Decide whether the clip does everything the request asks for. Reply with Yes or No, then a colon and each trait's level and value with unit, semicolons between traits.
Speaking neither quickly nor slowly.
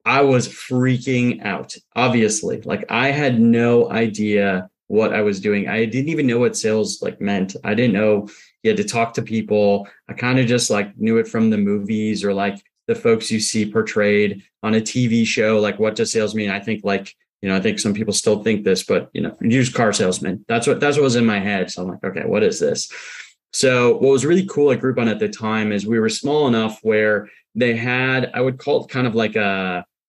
No: fast, 230 wpm